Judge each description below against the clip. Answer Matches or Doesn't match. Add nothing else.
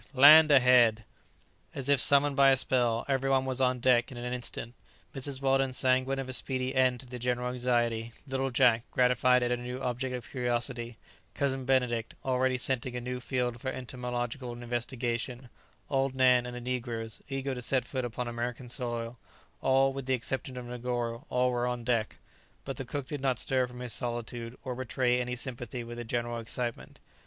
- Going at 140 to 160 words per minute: Doesn't match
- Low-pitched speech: Matches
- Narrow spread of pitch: Matches